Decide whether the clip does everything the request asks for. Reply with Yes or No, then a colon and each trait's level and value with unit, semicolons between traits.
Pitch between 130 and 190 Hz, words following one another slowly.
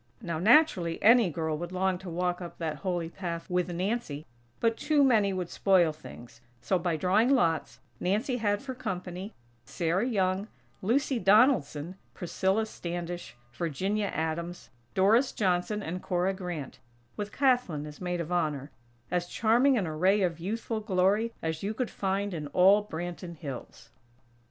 No: medium, 185 Hz; average, 150 wpm